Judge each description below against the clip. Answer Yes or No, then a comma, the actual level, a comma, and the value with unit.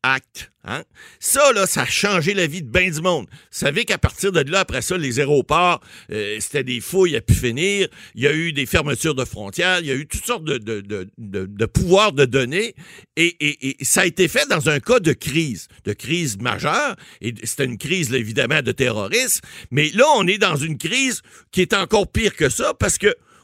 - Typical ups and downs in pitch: No, wide, 6.8 semitones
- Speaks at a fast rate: Yes, fast, 230 wpm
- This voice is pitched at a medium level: Yes, medium, 150 Hz